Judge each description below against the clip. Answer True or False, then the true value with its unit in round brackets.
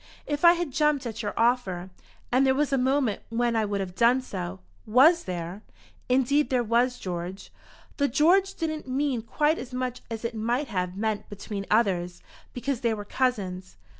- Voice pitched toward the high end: True (240 Hz)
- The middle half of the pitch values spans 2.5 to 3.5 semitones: False (5.1 semitones)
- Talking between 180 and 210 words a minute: True (185 wpm)